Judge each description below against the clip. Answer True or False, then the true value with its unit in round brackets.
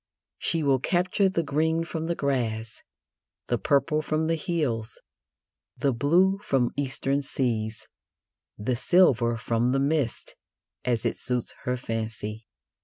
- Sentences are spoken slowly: True (130 wpm)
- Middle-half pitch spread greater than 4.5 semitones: True (5.3 semitones)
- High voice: False (135 Hz)